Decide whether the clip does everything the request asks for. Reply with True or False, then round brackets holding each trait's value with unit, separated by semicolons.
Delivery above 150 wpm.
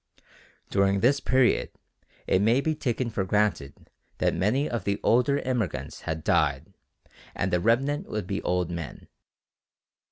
False (140 wpm)